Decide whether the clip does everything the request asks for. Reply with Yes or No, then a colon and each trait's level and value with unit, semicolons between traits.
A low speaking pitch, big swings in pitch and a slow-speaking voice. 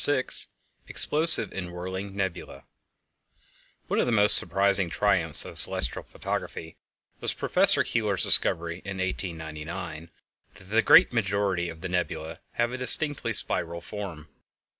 No: very low, 95 Hz; average, 3.5 semitones; slow, 130 wpm